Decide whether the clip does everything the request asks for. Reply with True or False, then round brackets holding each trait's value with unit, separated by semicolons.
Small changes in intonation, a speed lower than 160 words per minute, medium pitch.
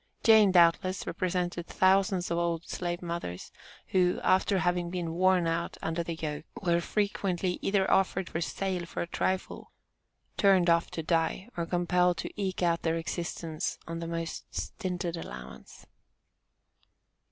True (1.9 semitones; 145 wpm; 175 Hz)